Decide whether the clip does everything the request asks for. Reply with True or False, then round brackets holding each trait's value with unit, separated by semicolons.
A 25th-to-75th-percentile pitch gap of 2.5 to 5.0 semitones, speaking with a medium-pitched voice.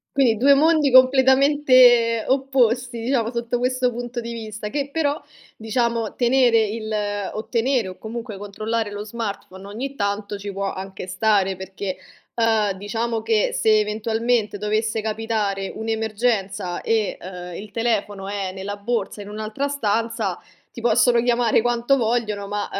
False (2.9 semitones; 225 Hz)